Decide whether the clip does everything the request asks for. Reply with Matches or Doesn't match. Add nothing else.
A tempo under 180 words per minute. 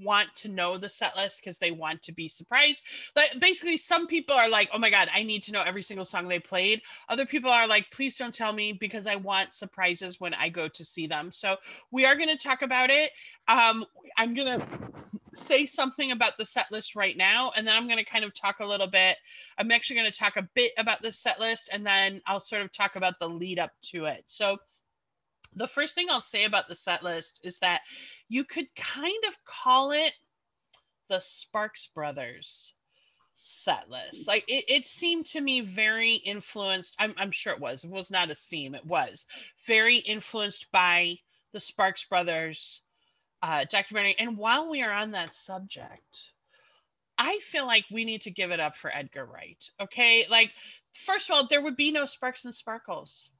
Doesn't match